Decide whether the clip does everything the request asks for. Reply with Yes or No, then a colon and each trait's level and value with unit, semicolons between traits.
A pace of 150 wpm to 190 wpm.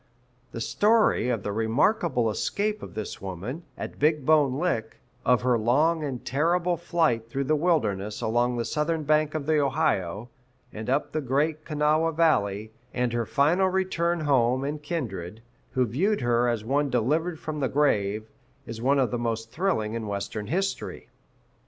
Yes: average, 170 wpm